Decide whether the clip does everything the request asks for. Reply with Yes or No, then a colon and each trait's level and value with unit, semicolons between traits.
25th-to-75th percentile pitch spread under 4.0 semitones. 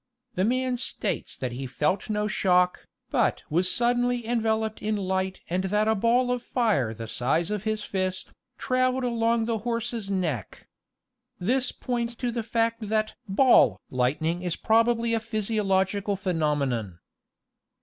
No: average, 4.4 semitones